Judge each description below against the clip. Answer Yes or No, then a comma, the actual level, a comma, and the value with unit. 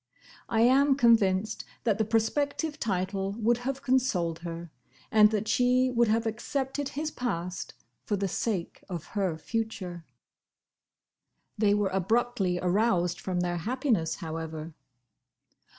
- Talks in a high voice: Yes, high, 215 Hz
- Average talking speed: No, slow, 125 wpm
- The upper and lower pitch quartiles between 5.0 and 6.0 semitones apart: Yes, average, 5.3 semitones